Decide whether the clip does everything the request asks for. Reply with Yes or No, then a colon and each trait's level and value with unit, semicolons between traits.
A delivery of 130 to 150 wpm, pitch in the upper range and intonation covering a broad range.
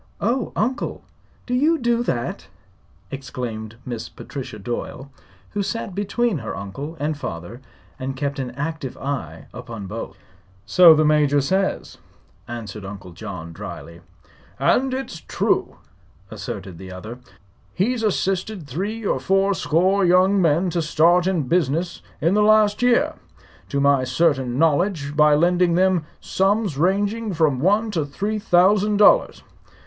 No: average, 140 wpm; medium, 165 Hz; wide, 7.3 semitones